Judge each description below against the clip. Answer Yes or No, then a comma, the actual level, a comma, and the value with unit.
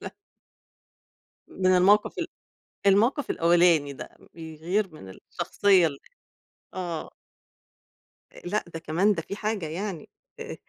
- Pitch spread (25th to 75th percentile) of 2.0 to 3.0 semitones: No, average, 4.0 semitones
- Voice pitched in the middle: Yes, medium, 180 Hz